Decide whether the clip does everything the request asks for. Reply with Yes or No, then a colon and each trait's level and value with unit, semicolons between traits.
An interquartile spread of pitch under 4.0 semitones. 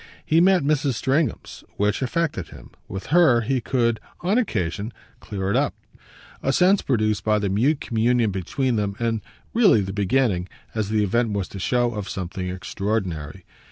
No: average, 5.3 semitones